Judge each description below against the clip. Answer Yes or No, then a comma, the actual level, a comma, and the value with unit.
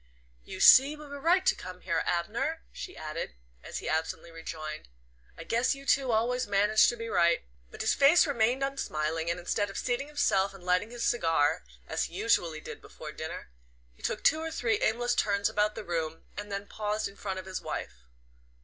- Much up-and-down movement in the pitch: Yes, wide, 6.5 semitones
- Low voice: No, high, 205 Hz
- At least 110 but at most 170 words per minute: No, average, 200 wpm